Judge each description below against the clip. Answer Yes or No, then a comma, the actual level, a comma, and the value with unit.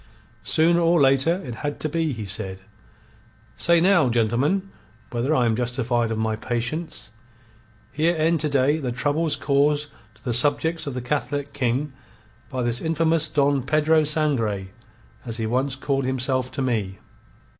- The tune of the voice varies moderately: Yes, average, 4.3 semitones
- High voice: No, medium, 140 Hz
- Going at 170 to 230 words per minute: No, average, 155 wpm